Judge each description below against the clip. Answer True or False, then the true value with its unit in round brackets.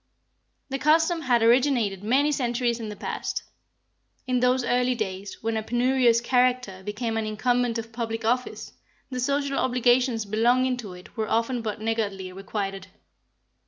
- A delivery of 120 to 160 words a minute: True (150 wpm)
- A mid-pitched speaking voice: False (235 Hz)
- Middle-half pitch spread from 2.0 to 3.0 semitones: True (2.7 semitones)